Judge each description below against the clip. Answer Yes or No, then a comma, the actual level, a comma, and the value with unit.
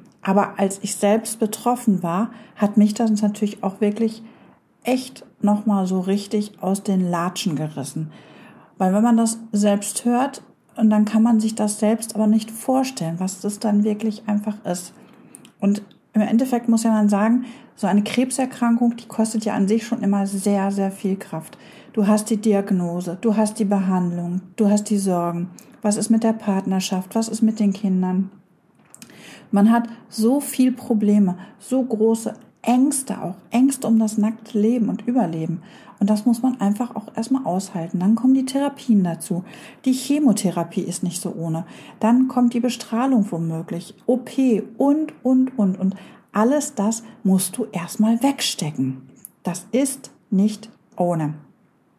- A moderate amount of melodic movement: Yes, average, 3.1 semitones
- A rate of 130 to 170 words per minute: Yes, average, 160 wpm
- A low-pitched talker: No, high, 215 Hz